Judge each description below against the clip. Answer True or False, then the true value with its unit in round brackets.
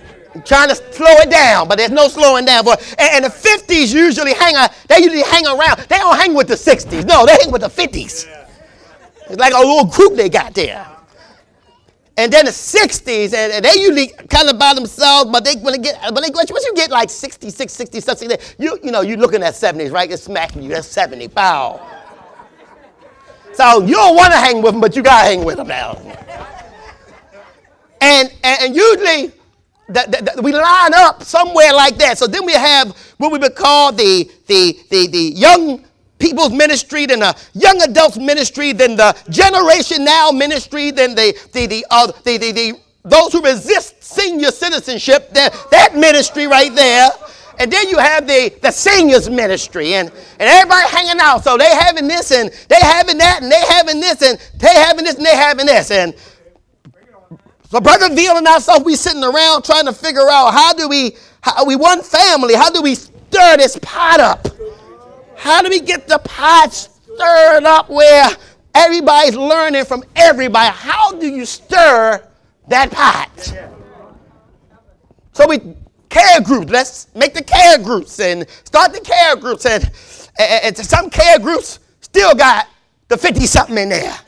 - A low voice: False (295 Hz)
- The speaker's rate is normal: True (190 wpm)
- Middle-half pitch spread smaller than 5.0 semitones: True (4.6 semitones)